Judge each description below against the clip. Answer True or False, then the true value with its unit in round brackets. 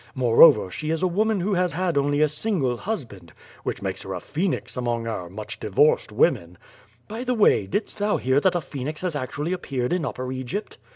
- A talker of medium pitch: True (150 Hz)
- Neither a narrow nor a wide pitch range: False (7.0 semitones)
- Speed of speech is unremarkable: False (210 wpm)